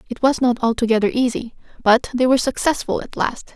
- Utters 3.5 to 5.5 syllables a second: No, 6.0 syllables/s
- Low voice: No, high, 245 Hz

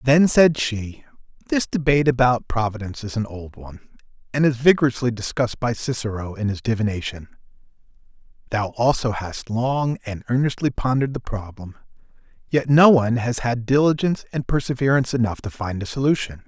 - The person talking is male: Yes, male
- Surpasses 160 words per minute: No, average, 155 wpm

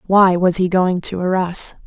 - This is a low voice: No, medium, 185 Hz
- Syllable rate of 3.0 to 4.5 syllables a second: Yes, 4.3 syllables/s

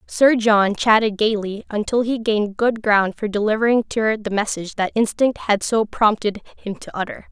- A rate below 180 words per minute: No, average, 190 wpm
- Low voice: No, high, 215 Hz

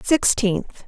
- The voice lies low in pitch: No, high, 225 Hz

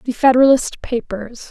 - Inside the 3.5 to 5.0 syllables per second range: Yes, 4.8 syllables/s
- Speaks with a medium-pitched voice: No, high, 245 Hz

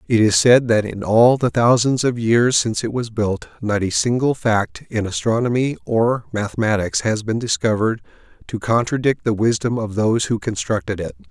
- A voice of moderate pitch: No, low, 115 Hz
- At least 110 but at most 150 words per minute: No, average, 180 wpm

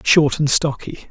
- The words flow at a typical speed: Yes, average, 160 wpm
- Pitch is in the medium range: Yes, medium, 145 Hz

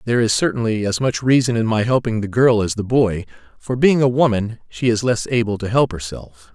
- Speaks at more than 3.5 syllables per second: Yes, 5.5 syllables/s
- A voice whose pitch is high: No, low, 115 Hz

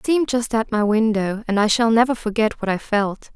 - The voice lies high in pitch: Yes, high, 220 Hz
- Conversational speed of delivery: No, fast, 250 wpm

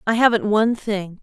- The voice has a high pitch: Yes, high, 215 Hz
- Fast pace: No, average, 195 wpm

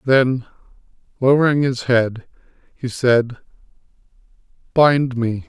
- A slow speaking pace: Yes, slow, 90 wpm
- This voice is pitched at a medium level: No, low, 125 Hz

